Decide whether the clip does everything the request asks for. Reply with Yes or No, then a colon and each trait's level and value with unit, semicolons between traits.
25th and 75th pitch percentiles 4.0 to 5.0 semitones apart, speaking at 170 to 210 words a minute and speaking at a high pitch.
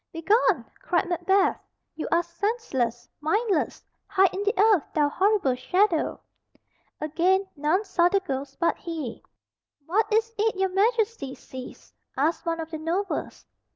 No: average, 4.6 semitones; average, 140 wpm; very high, 355 Hz